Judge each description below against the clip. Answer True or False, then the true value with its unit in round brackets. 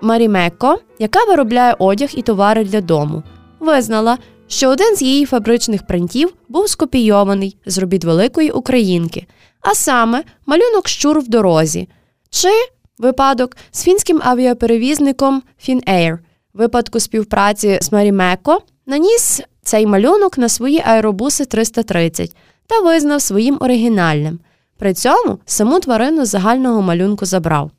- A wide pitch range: True (6.3 semitones)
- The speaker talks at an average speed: True (120 wpm)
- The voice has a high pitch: True (235 Hz)